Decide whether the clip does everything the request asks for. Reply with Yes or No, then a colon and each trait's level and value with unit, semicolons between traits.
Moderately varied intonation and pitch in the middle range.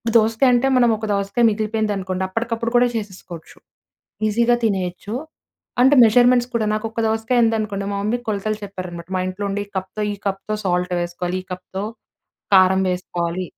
No: average, 3.4 semitones; high, 205 Hz